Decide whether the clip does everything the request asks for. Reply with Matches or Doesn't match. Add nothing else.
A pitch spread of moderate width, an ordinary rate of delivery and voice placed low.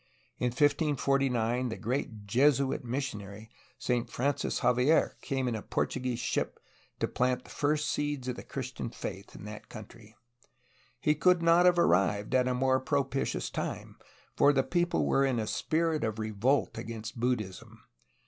Matches